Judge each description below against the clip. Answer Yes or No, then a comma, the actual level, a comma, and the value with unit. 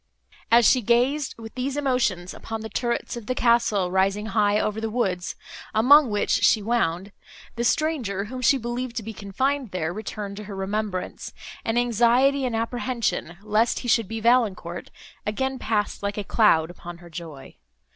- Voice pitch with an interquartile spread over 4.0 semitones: No, average, 3.4 semitones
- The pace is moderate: Yes, average, 170 wpm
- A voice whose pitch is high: Yes, high, 220 Hz